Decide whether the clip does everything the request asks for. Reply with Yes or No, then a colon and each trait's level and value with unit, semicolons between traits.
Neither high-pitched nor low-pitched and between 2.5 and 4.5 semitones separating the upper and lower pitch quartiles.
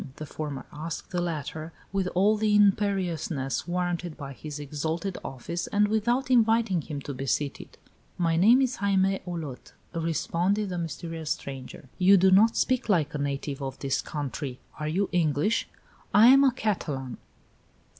No: medium, 170 Hz; wide, 5.5 semitones